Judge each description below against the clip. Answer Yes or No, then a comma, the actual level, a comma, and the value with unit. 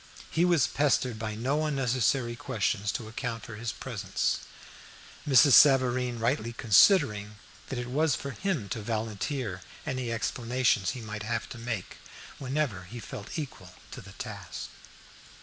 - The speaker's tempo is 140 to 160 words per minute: Yes, average, 145 wpm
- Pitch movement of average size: Yes, average, 3.6 semitones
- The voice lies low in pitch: Yes, low, 120 Hz